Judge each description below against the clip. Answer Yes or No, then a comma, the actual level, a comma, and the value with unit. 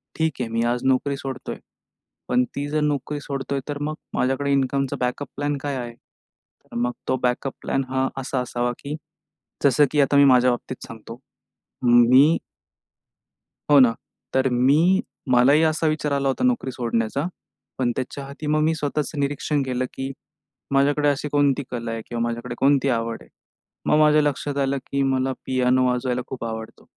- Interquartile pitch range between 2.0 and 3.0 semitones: Yes, narrow, 2.5 semitones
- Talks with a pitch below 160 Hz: Yes, low, 135 Hz